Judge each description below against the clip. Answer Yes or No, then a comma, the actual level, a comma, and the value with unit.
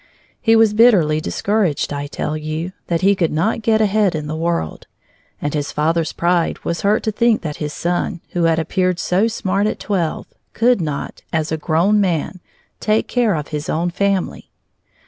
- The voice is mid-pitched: Yes, medium, 175 Hz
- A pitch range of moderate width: Yes, average, 4.9 semitones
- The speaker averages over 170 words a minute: Yes, average, 185 wpm